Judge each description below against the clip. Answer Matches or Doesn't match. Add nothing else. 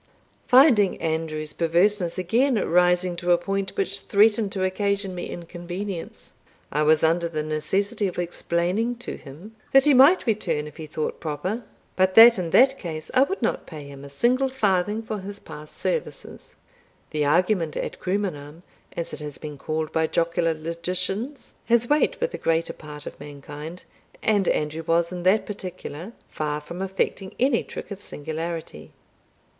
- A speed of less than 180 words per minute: Matches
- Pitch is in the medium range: Matches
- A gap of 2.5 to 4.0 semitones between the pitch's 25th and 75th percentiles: Doesn't match